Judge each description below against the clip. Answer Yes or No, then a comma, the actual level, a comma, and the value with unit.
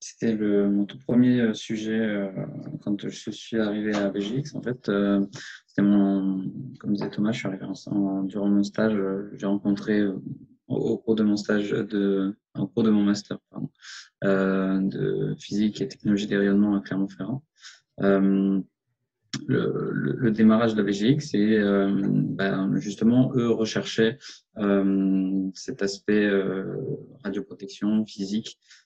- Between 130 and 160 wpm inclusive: Yes, average, 155 wpm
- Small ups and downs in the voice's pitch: Yes, narrow, 1.9 semitones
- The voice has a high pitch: No, low, 100 Hz